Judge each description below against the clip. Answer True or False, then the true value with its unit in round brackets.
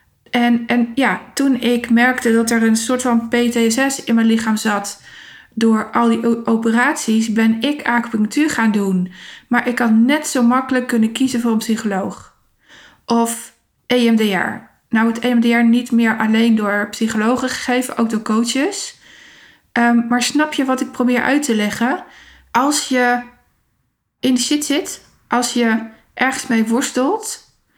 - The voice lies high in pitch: True (235 Hz)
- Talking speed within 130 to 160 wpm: True (155 wpm)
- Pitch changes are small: True (2.1 semitones)